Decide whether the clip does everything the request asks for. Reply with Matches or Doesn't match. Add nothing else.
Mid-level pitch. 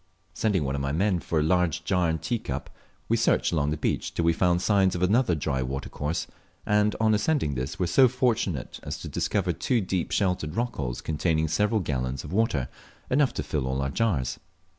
Doesn't match